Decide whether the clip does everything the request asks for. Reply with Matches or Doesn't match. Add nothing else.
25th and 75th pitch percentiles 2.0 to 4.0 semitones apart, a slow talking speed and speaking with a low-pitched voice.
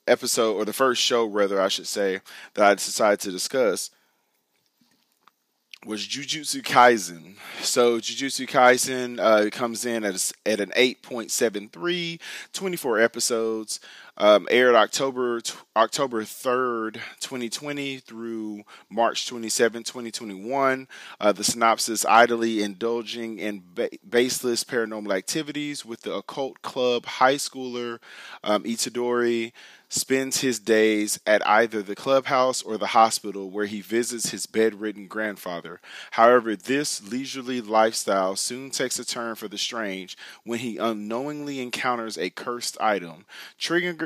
Matches